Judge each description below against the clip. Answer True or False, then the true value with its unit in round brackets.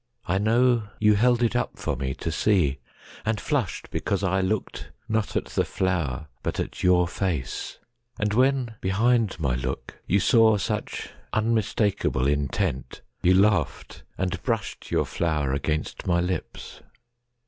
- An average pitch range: False (6.0 semitones)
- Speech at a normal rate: False (130 wpm)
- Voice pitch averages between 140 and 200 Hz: False (95 Hz)